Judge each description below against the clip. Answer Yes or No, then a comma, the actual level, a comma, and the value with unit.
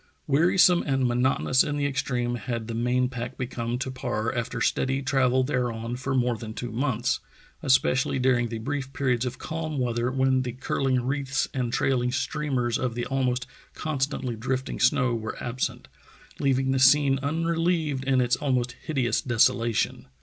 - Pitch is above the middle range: No, low, 130 Hz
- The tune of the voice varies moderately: No, narrow, 1.9 semitones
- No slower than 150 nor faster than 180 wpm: Yes, average, 160 wpm